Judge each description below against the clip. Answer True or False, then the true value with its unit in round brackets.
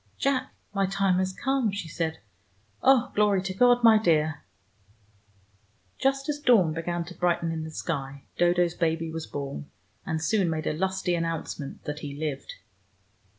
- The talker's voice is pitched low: False (175 Hz)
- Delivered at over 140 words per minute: True (155 wpm)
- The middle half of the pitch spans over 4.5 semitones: False (4.0 semitones)